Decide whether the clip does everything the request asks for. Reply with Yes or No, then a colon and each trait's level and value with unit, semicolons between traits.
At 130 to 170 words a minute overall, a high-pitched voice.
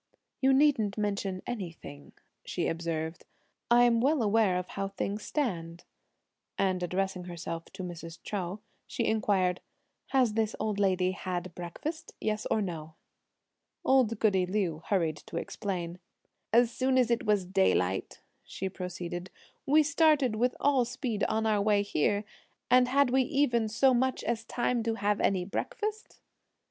Yes: average, 145 wpm; high, 205 Hz